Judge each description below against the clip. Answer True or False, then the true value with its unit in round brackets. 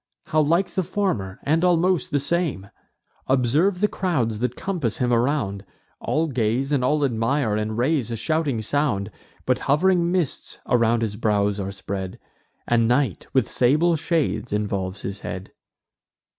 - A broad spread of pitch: True (6.8 semitones)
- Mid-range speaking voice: False (125 Hz)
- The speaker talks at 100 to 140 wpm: False (150 wpm)